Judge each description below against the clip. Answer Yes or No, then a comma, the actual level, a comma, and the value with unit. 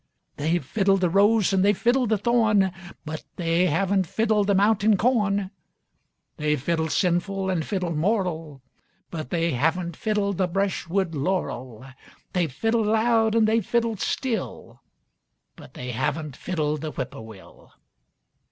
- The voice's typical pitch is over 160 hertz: Yes, medium, 185 Hz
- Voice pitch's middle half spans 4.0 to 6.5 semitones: Yes, average, 4.8 semitones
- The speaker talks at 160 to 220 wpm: No, slow, 135 wpm